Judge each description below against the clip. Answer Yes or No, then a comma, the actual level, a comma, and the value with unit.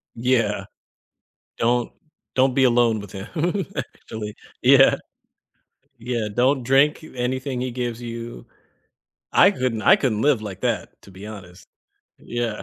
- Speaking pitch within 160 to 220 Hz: No, low, 120 Hz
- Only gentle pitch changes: No, average, 3.1 semitones